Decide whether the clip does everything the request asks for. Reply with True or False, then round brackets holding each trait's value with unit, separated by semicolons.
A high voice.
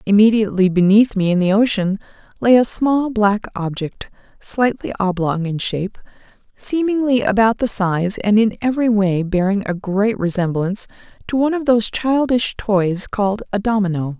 True (210 Hz)